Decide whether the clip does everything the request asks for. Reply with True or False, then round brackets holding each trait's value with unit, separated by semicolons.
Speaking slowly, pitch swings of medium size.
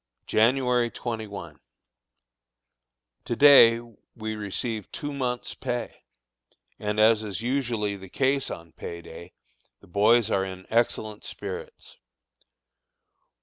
True (105 wpm; 3.4 semitones)